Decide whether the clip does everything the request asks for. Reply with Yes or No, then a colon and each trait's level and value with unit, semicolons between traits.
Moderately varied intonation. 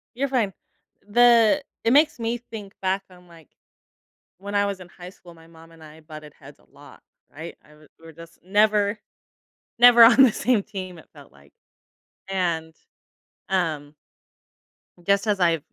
Yes: average, 4.8 semitones